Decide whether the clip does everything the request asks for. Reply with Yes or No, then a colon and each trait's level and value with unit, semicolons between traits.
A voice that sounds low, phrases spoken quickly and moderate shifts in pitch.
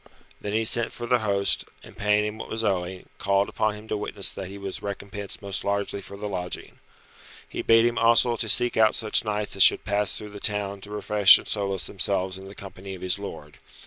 No: low, 100 Hz; fast, 225 wpm; narrow, 1.5 semitones